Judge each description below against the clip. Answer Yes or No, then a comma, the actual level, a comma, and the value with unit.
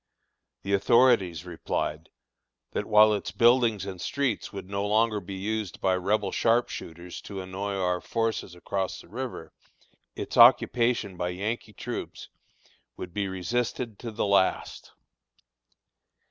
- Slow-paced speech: Yes, slow, 130 wpm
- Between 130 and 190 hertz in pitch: No, low, 100 Hz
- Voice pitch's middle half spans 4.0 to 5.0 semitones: No, average, 3.4 semitones